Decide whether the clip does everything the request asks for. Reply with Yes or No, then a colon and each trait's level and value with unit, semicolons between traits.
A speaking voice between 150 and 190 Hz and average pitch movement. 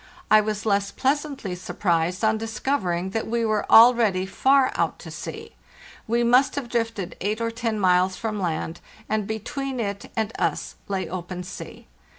No: high, 215 Hz; average, 3.7 semitones